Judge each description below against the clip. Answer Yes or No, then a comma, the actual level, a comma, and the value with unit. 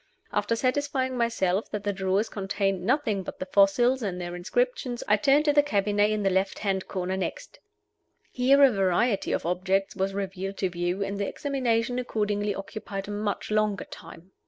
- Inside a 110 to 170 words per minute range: No, average, 180 wpm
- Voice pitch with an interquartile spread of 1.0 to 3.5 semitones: No, average, 4.0 semitones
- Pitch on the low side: No, high, 205 Hz